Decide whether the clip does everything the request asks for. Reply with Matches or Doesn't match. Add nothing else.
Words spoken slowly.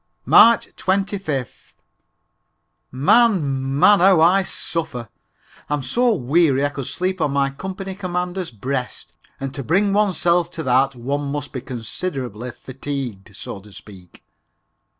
Matches